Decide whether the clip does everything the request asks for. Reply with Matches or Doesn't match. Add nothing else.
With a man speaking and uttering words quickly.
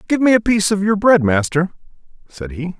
Matches